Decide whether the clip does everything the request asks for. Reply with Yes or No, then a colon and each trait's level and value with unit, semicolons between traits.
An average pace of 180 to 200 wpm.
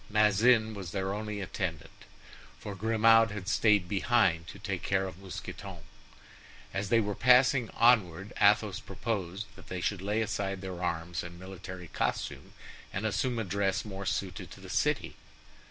No: average, 155 wpm